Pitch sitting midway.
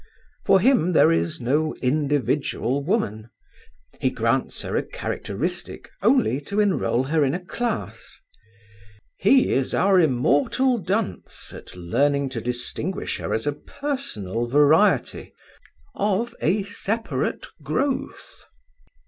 Yes: medium, 155 Hz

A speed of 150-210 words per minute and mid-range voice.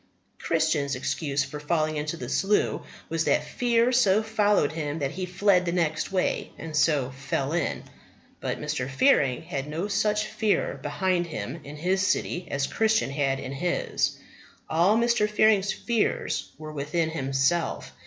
Yes: average, 155 wpm; medium, 165 Hz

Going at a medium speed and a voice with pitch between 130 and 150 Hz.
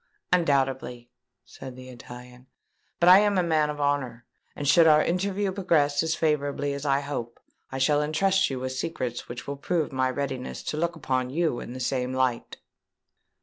Yes: average, 180 wpm; medium, 140 Hz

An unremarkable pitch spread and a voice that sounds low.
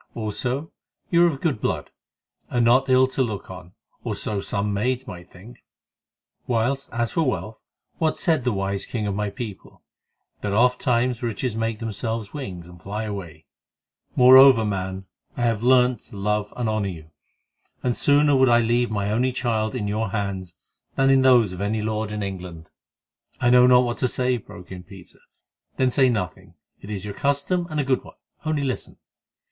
Yes: average, 4.2 semitones; low, 115 Hz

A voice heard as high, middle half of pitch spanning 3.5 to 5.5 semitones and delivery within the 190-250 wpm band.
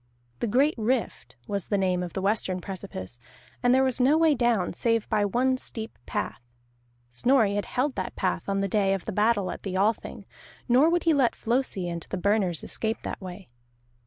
Yes: high, 210 Hz; average, 4.8 semitones; average, 195 wpm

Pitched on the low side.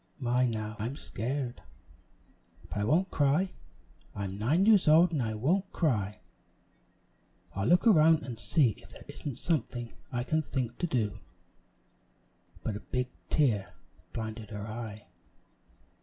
Yes: low, 125 Hz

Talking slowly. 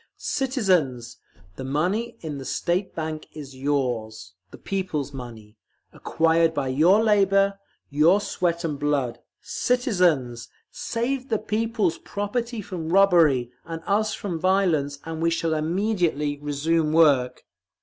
Yes: slow, 125 wpm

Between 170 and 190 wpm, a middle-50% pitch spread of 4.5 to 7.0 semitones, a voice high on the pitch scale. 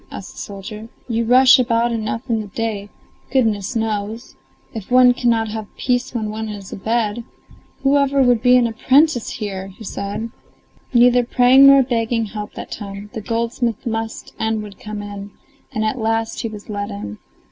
No: average, 175 wpm; narrow, 2.6 semitones; high, 225 Hz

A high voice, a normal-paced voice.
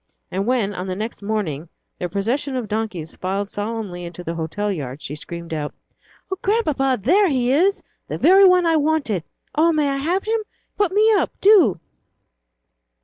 Yes: high, 225 Hz; average, 175 wpm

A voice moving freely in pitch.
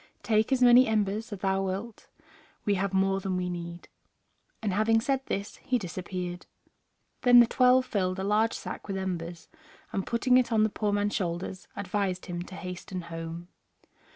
No: average, 3.4 semitones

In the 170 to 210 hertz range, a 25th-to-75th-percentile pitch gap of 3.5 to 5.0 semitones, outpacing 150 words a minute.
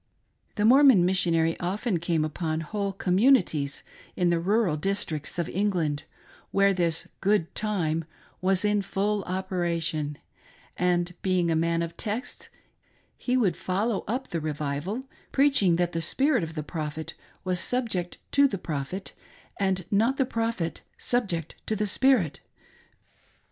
No: medium, 185 Hz; average, 4.2 semitones; average, 145 wpm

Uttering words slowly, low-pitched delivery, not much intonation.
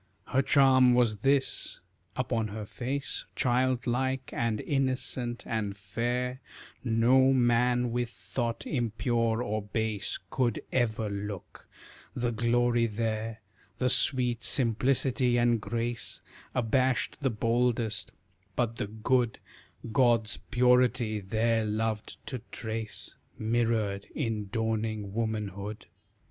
Yes: slow, 105 wpm; low, 115 Hz; narrow, 2.3 semitones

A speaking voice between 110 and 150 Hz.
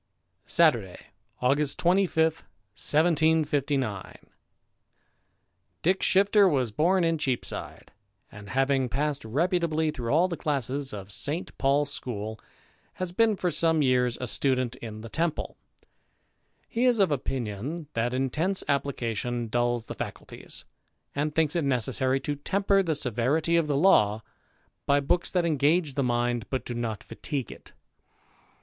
Yes: medium, 140 Hz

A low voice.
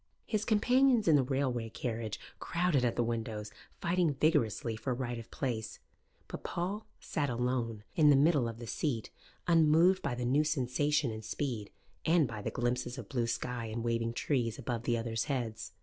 Yes: low, 125 Hz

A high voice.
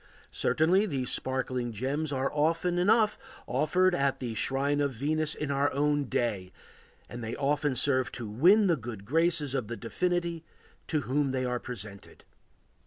No: medium, 140 Hz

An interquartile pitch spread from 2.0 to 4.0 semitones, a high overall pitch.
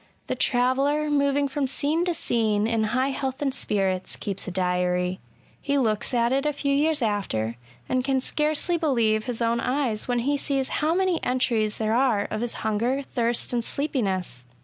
No: average, 4.7 semitones; very high, 250 Hz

